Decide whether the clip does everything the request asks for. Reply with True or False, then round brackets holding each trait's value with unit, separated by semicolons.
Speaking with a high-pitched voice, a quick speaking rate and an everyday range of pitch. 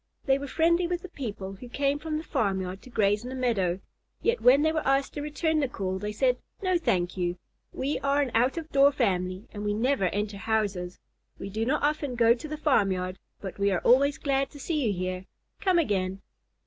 False (245 Hz; 220 wpm; 6.7 semitones)